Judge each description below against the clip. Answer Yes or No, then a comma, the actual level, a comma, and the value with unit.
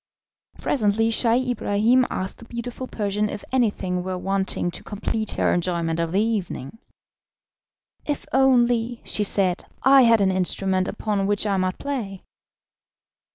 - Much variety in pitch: No, average, 3.9 semitones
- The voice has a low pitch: No, high, 210 Hz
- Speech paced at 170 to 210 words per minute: No, average, 140 wpm